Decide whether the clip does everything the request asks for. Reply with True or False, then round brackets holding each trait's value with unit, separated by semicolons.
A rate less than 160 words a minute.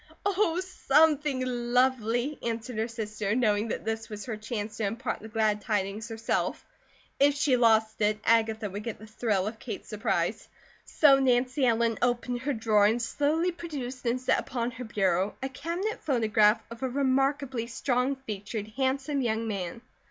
False (165 wpm)